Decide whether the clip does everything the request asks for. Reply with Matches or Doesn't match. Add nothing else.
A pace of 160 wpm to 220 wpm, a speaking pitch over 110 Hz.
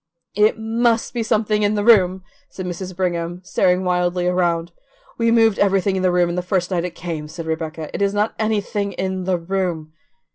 Matches